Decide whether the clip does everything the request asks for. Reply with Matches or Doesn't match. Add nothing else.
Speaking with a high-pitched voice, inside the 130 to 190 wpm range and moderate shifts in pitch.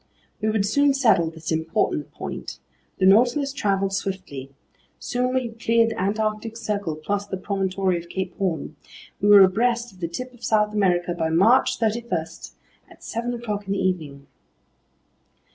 Matches